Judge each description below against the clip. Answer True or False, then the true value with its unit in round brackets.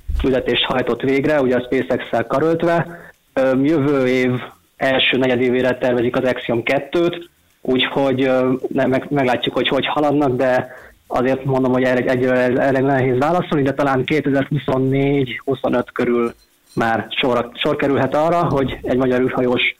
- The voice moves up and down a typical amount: False (1.7 semitones)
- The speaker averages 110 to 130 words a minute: True (125 wpm)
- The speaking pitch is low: True (130 Hz)